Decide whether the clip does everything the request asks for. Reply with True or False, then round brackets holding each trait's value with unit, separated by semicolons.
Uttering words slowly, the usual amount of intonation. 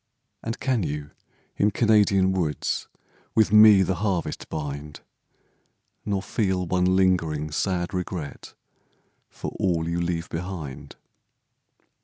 True (110 wpm; 3.3 semitones)